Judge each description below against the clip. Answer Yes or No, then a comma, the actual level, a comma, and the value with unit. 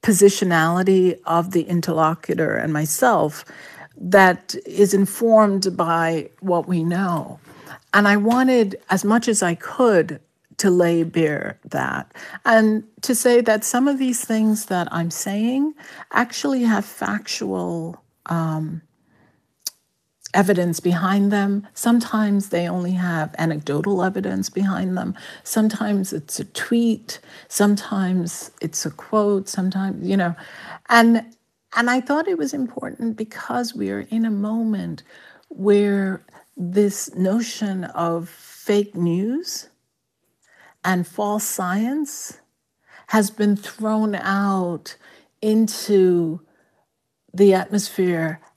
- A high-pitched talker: Yes, high, 200 Hz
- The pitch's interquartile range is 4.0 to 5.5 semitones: Yes, average, 4.3 semitones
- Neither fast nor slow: No, slow, 110 wpm